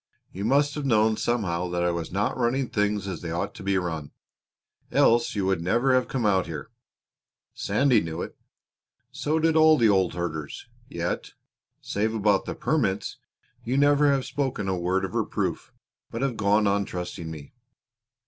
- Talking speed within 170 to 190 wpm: Yes, average, 175 wpm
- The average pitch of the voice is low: Yes, low, 105 Hz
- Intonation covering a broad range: Yes, wide, 6.3 semitones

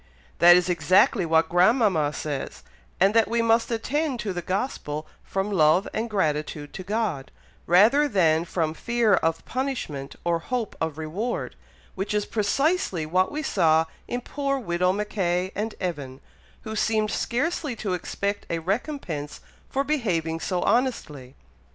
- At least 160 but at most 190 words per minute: No, average, 145 wpm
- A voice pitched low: No, high, 190 Hz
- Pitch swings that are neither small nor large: No, wide, 5.9 semitones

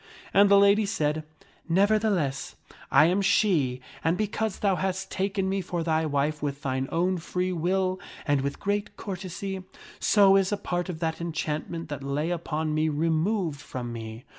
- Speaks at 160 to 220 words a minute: Yes, average, 170 wpm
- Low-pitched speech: No, medium, 175 Hz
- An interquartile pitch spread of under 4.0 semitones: No, average, 4.3 semitones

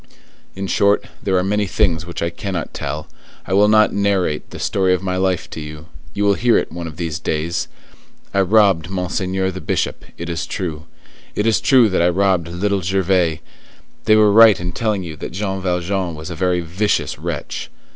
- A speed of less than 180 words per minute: No, average, 195 wpm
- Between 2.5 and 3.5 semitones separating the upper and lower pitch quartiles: Yes, average, 3.0 semitones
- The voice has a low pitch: Yes, very low, 95 Hz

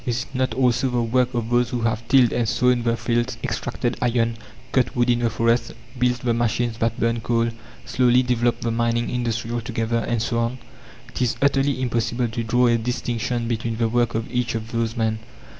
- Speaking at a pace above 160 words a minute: Yes, fast, 205 wpm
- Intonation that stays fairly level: Yes, narrow, 1.2 semitones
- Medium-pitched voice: No, low, 120 Hz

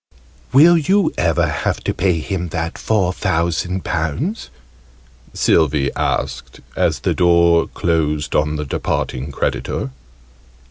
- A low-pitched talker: Yes, very low, 85 Hz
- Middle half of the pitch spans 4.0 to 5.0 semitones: No, average, 3.6 semitones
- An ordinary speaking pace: No, slow, 120 wpm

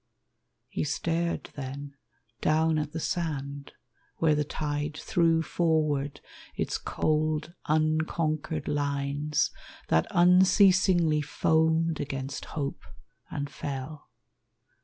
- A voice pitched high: No, medium, 155 Hz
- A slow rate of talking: Yes, slow, 95 wpm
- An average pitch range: No, narrow, 2.1 semitones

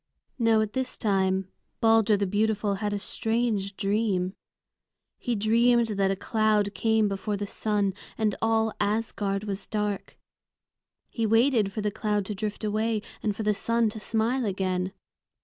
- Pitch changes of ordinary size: No, narrow, 1.9 semitones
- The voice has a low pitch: No, high, 210 Hz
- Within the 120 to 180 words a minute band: Yes, average, 155 wpm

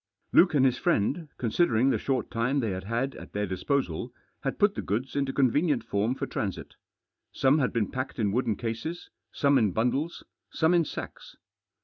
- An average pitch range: Yes, average, 4.3 semitones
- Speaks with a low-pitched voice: Yes, low, 130 Hz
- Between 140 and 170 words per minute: No, average, 185 wpm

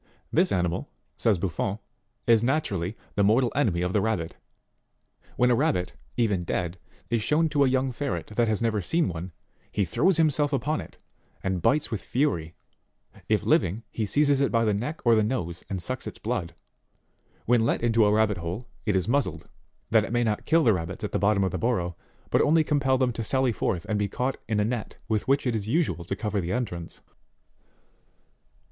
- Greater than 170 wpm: Yes, average, 200 wpm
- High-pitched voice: No, low, 110 Hz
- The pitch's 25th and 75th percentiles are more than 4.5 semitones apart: Yes, average, 5.2 semitones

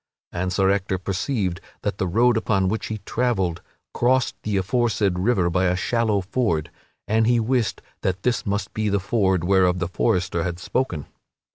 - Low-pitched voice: Yes, low, 100 Hz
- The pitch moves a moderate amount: Yes, average, 3.8 semitones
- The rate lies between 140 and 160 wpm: No, average, 170 wpm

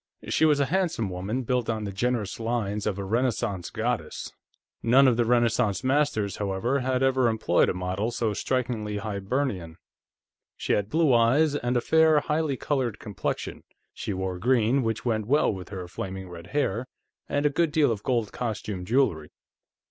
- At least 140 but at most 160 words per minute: No, average, 170 wpm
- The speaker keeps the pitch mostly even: No, average, 4.7 semitones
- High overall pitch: No, low, 115 Hz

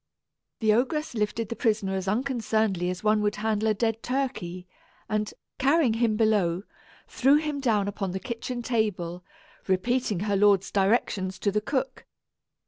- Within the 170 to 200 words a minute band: No, average, 150 wpm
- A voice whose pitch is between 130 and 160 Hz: No, high, 215 Hz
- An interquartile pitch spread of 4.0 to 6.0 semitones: No, average, 3.6 semitones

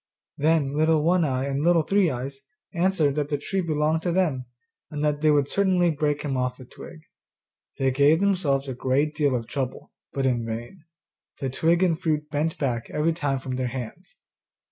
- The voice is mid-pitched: Yes, medium, 150 Hz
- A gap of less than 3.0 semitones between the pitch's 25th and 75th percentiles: No, average, 3.4 semitones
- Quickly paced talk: No, average, 190 wpm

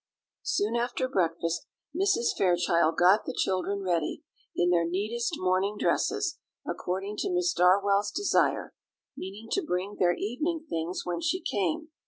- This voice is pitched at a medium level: No, high, 195 Hz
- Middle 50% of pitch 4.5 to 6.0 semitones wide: Yes, average, 5.0 semitones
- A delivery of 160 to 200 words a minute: No, average, 140 wpm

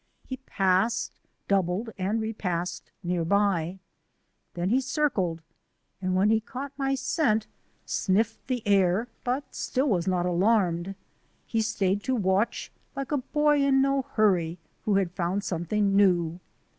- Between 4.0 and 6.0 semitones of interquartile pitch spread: Yes, average, 5.1 semitones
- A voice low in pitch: No, high, 200 Hz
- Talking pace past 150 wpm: No, average, 140 wpm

